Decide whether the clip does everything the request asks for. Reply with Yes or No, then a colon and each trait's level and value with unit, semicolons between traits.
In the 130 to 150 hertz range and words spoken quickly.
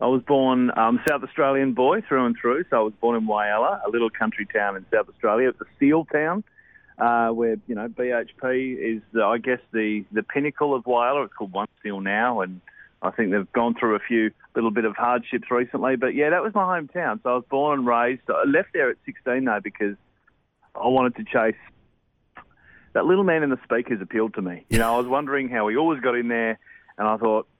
No: low, 120 Hz; fast, 230 wpm